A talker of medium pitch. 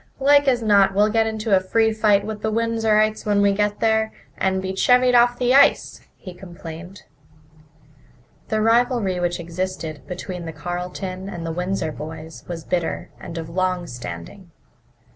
No: high, 195 Hz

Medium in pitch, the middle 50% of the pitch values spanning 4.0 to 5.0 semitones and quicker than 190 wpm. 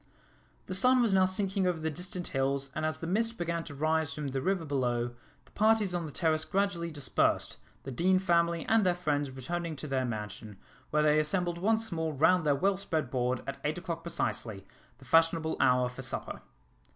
Yes: medium, 160 Hz; average, 4.7 semitones; average, 200 wpm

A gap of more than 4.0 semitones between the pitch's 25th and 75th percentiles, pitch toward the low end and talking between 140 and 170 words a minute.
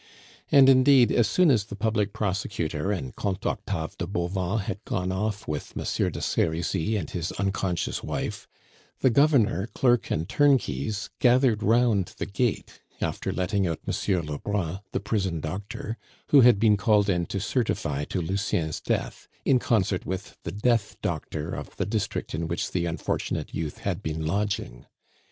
Yes: average, 4.5 semitones; low, 100 Hz; average, 160 wpm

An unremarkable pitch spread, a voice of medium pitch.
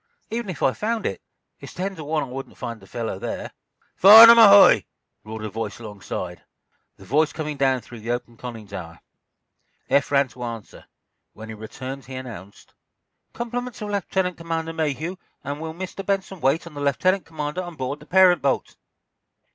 No: wide, 7.4 semitones; medium, 145 Hz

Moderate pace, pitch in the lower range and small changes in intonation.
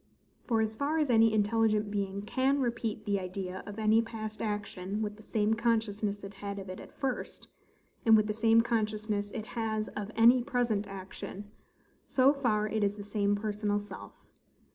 No: average, 180 wpm; high, 215 Hz; narrow, 1.8 semitones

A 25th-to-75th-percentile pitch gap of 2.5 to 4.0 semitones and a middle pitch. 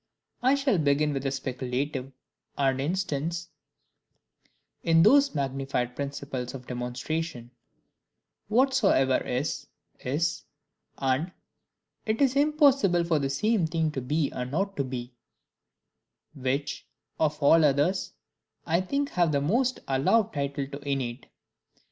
No: average, 5.2 semitones; medium, 145 Hz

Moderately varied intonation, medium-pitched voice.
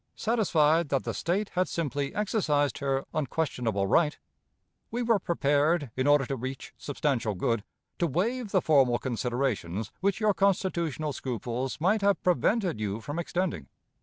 No: wide, 6.1 semitones; medium, 150 Hz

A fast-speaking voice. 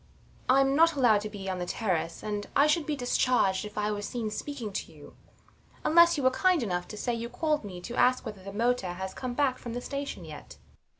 Yes: fast, 230 wpm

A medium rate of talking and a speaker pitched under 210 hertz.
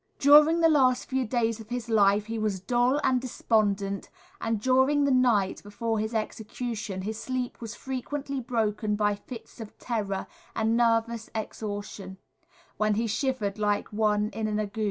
No: average, 160 wpm; high, 225 Hz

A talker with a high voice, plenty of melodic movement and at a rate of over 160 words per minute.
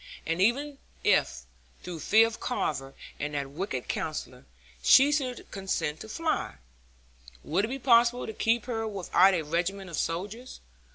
No: high, 200 Hz; wide, 6.4 semitones; average, 155 wpm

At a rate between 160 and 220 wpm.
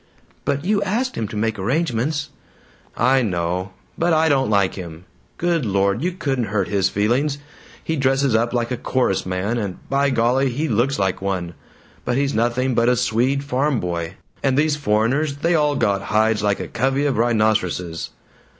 Yes: average, 175 wpm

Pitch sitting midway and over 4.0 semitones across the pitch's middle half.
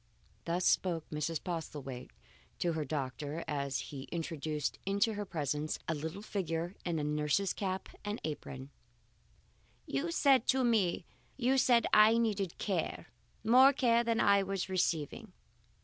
Yes: medium, 170 Hz; average, 5.0 semitones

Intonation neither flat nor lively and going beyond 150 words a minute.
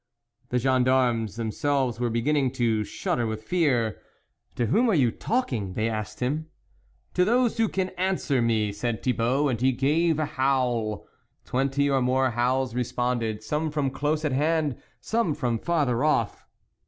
Yes: average, 4.5 semitones; average, 170 wpm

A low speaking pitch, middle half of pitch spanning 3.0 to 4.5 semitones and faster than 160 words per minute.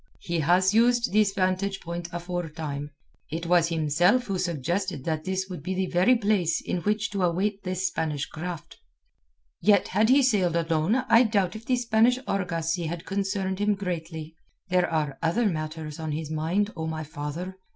No: medium, 180 Hz; average, 3.8 semitones; average, 175 wpm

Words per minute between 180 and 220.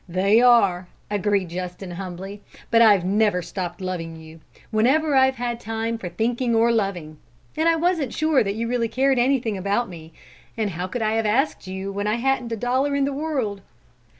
Yes: average, 190 wpm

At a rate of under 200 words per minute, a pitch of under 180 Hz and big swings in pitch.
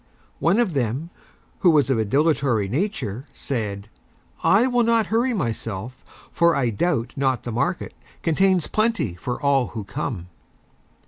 Yes: average, 145 wpm; medium, 140 Hz; wide, 7.7 semitones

